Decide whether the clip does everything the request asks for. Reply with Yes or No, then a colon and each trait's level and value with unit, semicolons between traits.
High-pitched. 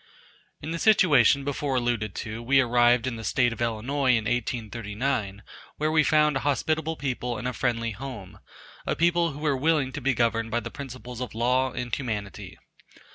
No: low, 125 Hz